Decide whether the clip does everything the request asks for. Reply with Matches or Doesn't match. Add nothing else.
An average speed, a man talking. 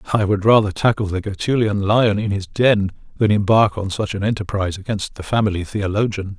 Matches